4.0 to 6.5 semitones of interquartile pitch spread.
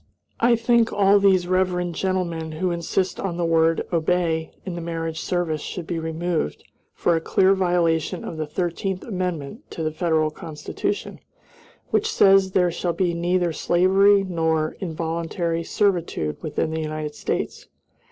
No: narrow, 2.4 semitones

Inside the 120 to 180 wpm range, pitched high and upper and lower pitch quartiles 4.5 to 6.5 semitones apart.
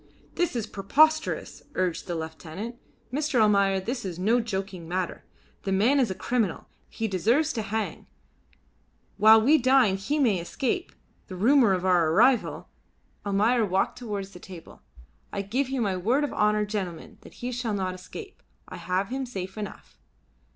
Yes: average, 165 wpm; high, 210 Hz; average, 4.9 semitones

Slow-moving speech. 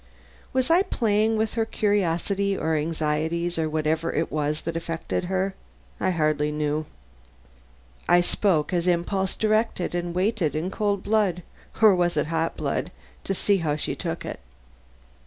No: average, 155 wpm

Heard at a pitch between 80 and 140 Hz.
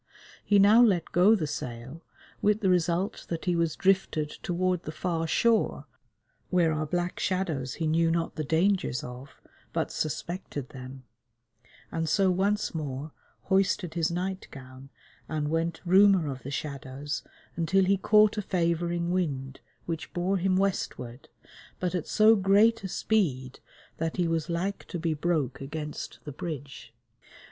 No: medium, 170 Hz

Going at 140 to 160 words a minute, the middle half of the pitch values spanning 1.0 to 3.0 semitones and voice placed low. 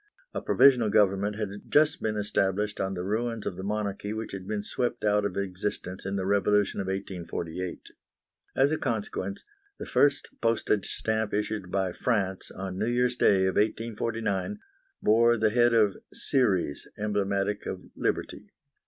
Yes: average, 155 wpm; narrow, 2.6 semitones; low, 105 Hz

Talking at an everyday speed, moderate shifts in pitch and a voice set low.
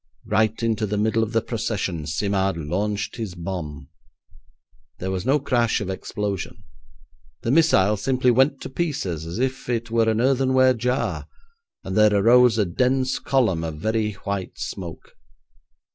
Yes: average, 150 wpm; average, 4.7 semitones; low, 110 Hz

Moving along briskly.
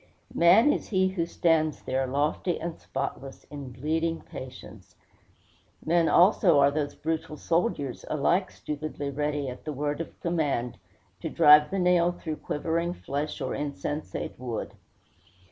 No: average, 140 wpm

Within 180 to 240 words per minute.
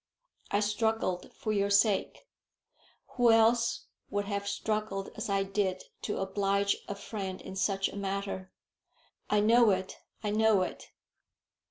No: average, 140 wpm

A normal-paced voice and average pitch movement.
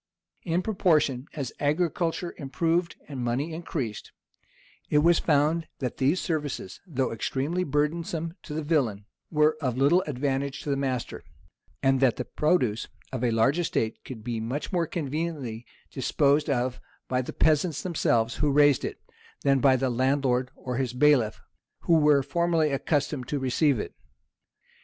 Yes: average, 150 wpm; average, 3.7 semitones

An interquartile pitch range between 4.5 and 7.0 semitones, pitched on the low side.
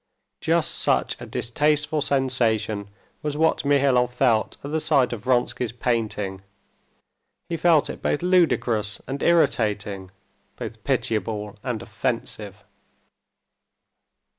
Yes: average, 4.9 semitones; low, 125 Hz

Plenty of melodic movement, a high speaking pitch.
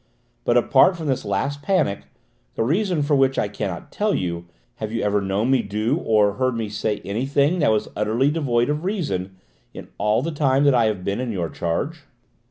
No: wide, 5.8 semitones; low, 120 Hz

